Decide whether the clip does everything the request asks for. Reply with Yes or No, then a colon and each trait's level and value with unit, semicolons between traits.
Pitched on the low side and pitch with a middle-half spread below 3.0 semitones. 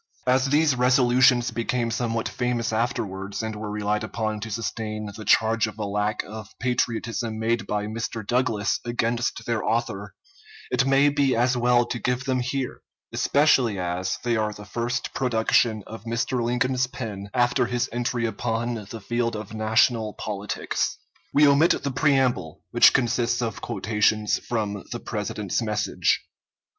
Yes: low, 115 Hz; narrow, 2.4 semitones